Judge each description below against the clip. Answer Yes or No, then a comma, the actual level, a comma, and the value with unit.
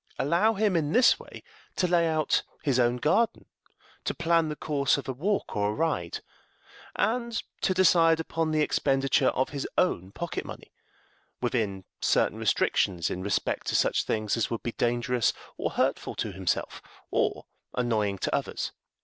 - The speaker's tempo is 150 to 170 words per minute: Yes, average, 165 wpm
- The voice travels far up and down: Yes, wide, 6.6 semitones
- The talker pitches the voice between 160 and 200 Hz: No, medium, 140 Hz